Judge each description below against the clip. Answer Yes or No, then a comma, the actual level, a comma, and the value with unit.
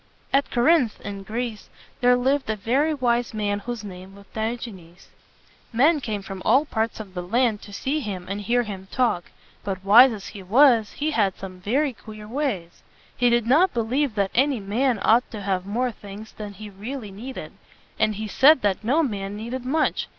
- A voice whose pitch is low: No, high, 220 Hz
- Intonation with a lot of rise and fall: No, average, 4.1 semitones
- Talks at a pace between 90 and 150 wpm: No, fast, 205 wpm